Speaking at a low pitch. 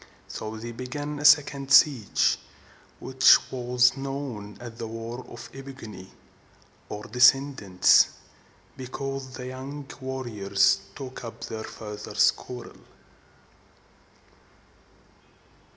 Yes: low, 125 Hz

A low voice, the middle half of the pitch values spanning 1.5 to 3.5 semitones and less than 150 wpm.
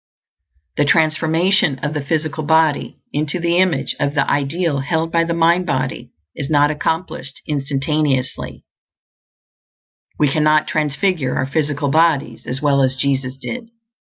No: medium, 150 Hz; average, 2.7 semitones; slow, 135 wpm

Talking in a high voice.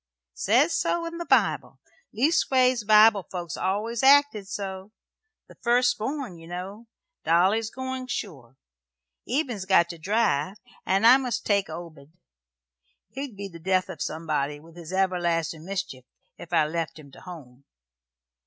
Yes: high, 195 Hz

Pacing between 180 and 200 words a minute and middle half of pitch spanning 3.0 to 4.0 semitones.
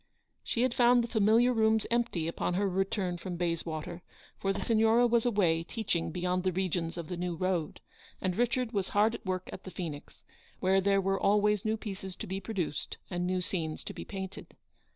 Yes: average, 195 wpm; average, 3.6 semitones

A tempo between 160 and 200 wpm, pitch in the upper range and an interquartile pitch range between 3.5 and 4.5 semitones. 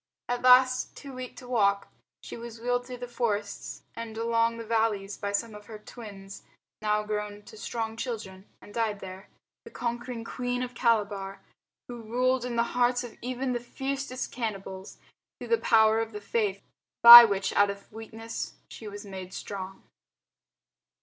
No: average, 170 wpm; high, 225 Hz; average, 3.1 semitones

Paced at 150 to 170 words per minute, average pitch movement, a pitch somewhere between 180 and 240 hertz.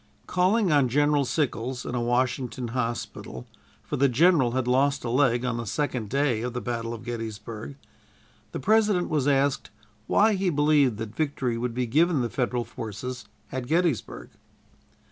No: average, 165 wpm; average, 3.7 semitones; low, 130 Hz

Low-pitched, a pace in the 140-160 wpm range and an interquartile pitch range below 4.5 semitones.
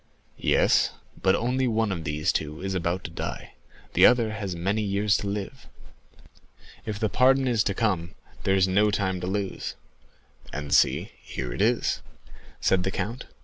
No: low, 100 Hz; average, 170 wpm; average, 3.2 semitones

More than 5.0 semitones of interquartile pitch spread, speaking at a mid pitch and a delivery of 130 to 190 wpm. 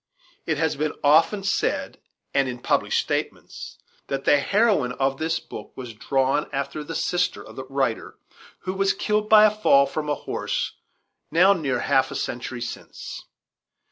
Yes: wide, 5.6 semitones; medium, 150 Hz; average, 165 wpm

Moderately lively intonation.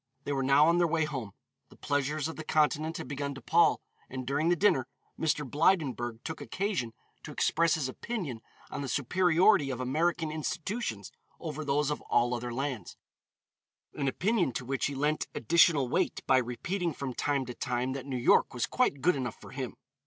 Yes: average, 4.1 semitones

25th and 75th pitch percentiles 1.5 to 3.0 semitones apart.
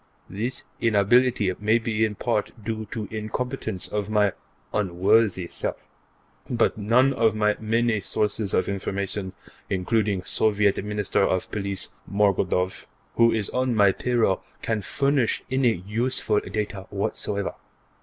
Yes: narrow, 2.5 semitones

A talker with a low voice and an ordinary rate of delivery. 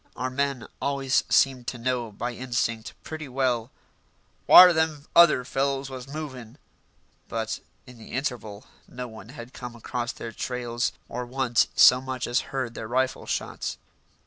Yes: low, 125 Hz; average, 150 wpm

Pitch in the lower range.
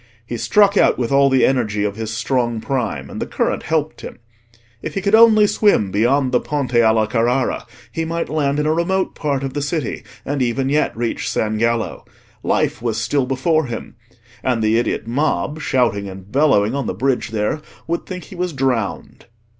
Yes: low, 130 Hz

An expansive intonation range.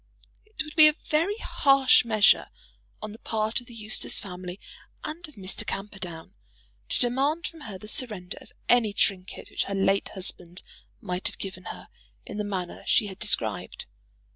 Yes: wide, 5.8 semitones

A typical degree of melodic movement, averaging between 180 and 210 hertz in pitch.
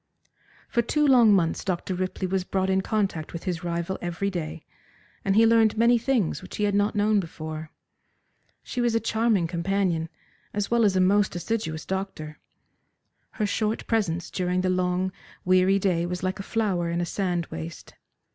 Yes: average, 3.4 semitones; high, 190 Hz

